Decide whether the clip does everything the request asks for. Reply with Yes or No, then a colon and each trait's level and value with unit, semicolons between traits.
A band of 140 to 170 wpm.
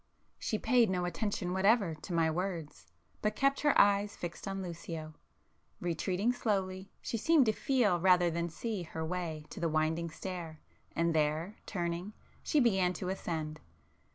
Yes: average, 155 wpm